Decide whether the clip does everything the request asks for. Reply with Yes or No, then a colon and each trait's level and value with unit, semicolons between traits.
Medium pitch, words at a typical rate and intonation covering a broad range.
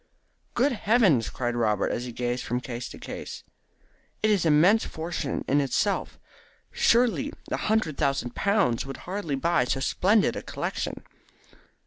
Yes: medium, 155 Hz; average, 150 wpm; wide, 8.8 semitones